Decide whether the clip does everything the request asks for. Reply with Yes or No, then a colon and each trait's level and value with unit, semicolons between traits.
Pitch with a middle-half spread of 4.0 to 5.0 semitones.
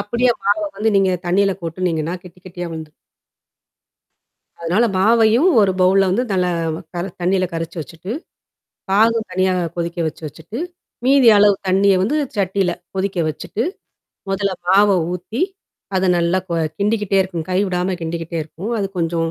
No: average, 3.0 semitones